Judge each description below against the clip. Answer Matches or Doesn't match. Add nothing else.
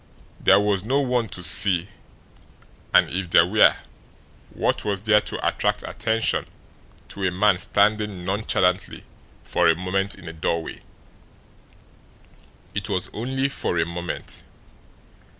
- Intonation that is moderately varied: Matches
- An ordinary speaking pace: Doesn't match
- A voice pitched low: Matches